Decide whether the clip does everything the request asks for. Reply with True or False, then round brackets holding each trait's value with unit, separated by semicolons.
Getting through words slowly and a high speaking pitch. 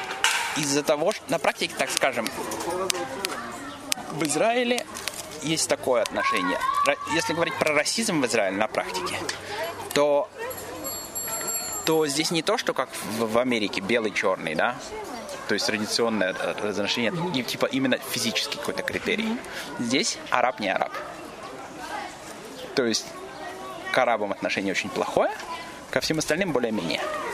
False (120 wpm; 155 Hz)